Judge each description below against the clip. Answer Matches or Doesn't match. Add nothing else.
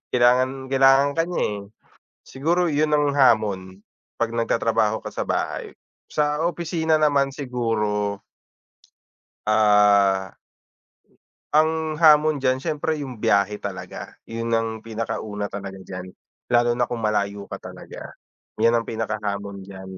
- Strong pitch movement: Matches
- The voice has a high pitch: Doesn't match